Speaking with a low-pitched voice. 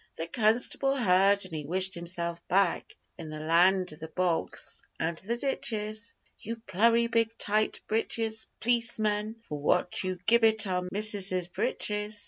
No: high, 205 Hz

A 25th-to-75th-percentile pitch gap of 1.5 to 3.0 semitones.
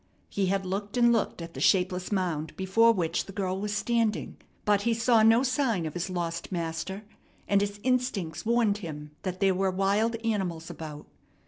No: average, 3.9 semitones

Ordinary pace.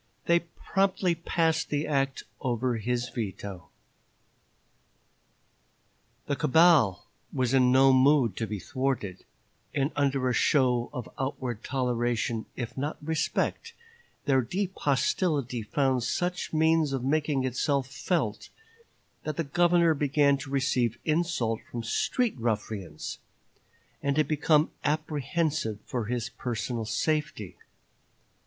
No: slow, 115 wpm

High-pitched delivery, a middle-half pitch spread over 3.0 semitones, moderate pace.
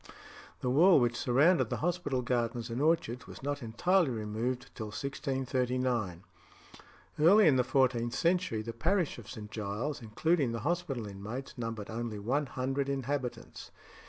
No: low, 125 Hz; average, 3.9 semitones; average, 145 wpm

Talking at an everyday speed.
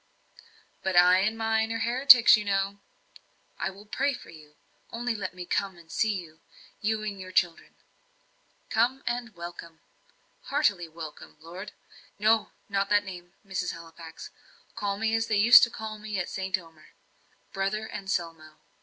Yes: average, 160 wpm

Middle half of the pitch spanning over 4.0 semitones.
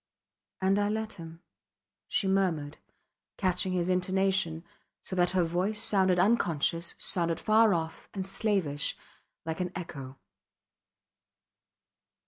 No: average, 2.7 semitones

